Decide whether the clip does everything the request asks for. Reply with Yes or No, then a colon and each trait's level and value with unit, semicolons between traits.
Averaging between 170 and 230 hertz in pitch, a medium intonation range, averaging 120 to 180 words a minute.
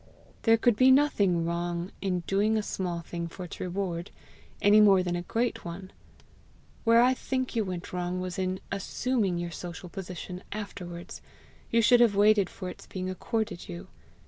Yes: high, 190 Hz; average, 3.5 semitones; average, 170 wpm